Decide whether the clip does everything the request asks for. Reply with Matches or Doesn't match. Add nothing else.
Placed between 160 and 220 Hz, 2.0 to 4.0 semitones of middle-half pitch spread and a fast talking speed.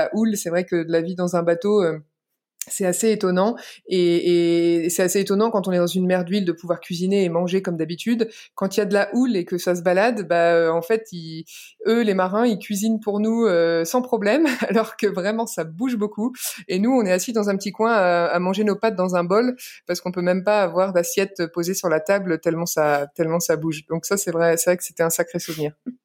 Matches